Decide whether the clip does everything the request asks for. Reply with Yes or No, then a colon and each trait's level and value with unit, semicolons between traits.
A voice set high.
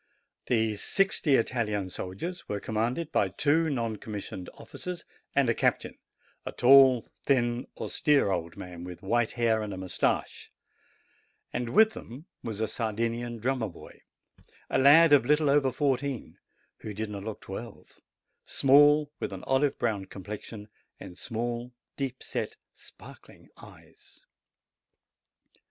No: low, 120 Hz